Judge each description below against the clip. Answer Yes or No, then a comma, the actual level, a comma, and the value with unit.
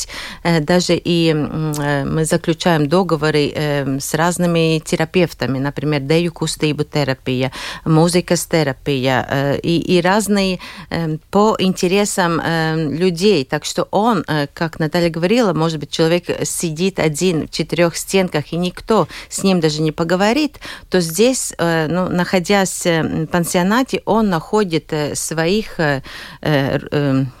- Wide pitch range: No, average, 3.3 semitones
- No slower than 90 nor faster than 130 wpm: Yes, slow, 110 wpm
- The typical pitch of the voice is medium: Yes, medium, 165 Hz